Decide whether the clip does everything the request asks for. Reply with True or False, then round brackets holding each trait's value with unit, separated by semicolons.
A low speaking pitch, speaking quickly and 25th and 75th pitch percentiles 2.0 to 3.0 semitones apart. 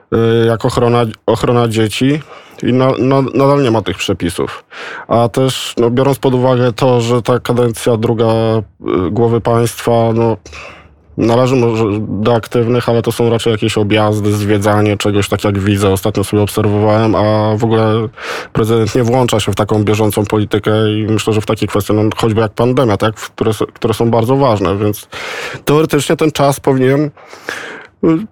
True (115 Hz; 165 wpm; 2.7 semitones)